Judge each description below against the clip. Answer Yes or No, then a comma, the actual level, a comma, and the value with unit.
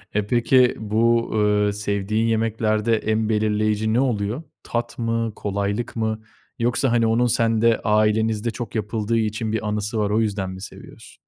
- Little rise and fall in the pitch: Yes, narrow, 1.6 semitones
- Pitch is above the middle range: No, low, 110 Hz